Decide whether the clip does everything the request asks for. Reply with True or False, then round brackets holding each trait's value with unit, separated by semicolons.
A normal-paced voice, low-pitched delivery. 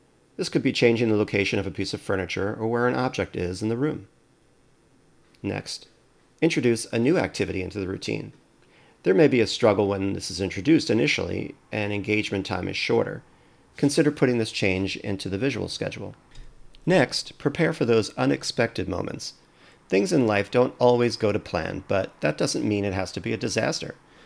True (185 wpm; 105 Hz)